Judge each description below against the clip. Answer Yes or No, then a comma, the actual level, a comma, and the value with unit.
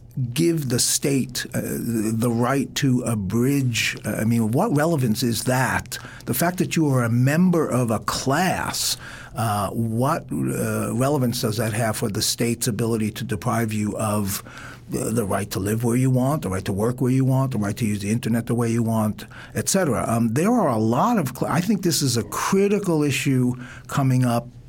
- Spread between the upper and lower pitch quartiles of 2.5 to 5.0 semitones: Yes, average, 3.1 semitones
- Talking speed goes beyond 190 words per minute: Yes, fast, 205 wpm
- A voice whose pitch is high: No, low, 120 Hz